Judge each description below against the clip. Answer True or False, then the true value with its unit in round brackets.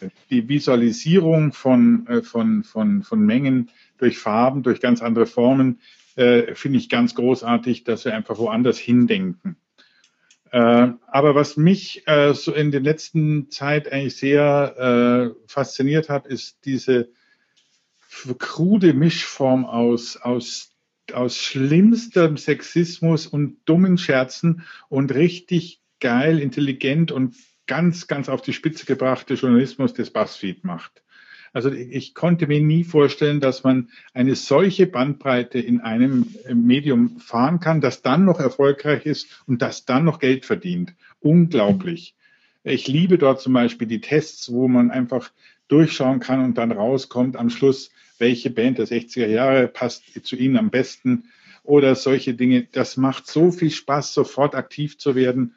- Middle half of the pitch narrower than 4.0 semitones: False (4.7 semitones)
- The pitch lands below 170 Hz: True (140 Hz)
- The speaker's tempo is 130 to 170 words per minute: True (145 wpm)